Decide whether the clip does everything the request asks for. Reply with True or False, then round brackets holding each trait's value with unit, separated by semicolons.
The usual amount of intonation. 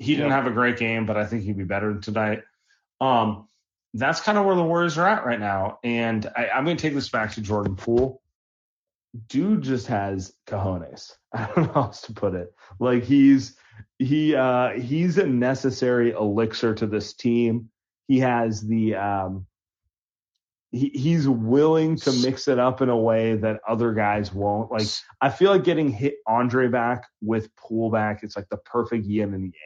True (3.8 semitones)